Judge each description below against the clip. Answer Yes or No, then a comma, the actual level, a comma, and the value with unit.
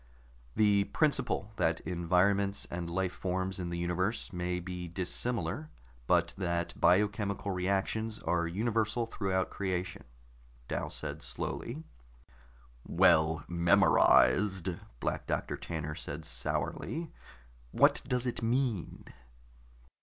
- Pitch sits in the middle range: No, very low, 95 Hz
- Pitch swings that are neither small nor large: Yes, average, 3.5 semitones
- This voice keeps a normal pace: No, slow, 105 wpm